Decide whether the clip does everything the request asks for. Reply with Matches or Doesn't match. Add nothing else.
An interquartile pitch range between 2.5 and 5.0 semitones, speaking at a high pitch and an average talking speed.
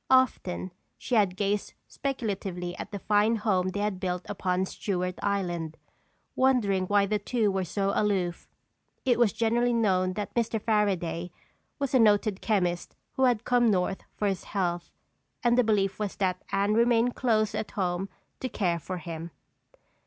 Matches